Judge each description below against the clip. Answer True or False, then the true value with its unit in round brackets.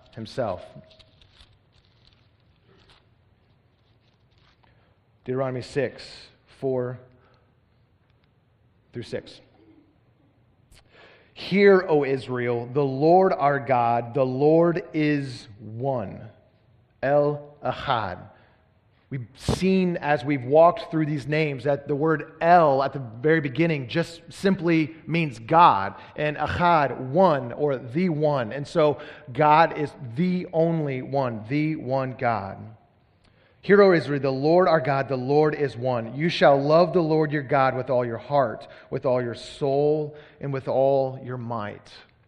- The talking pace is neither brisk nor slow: False (120 wpm)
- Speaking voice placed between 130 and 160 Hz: True (135 Hz)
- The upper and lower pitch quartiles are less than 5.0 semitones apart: True (4.4 semitones)